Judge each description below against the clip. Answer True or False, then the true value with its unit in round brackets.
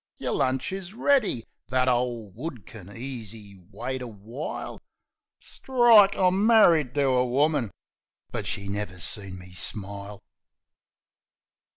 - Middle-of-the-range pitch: False (125 Hz)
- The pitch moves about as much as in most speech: False (7.5 semitones)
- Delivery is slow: True (120 wpm)